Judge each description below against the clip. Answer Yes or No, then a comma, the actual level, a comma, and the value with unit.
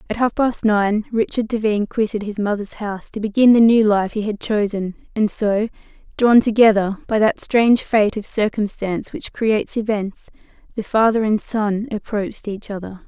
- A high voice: Yes, high, 215 Hz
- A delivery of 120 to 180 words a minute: Yes, average, 175 wpm